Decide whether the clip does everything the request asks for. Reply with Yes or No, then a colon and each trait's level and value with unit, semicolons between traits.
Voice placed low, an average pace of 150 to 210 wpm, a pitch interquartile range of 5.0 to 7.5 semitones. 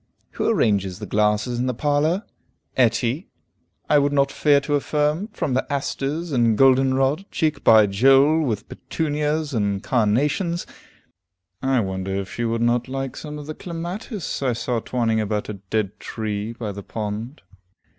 Yes: low, 130 Hz; average, 160 wpm; average, 5.3 semitones